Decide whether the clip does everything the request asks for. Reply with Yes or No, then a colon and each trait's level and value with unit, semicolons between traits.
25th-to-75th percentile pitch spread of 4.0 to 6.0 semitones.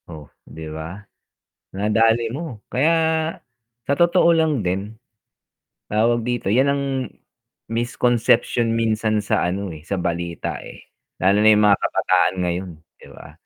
Yes: average, 4.6 semitones